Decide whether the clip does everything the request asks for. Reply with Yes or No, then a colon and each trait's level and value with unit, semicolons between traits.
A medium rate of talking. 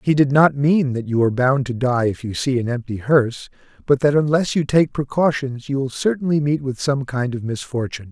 No: fast, 230 wpm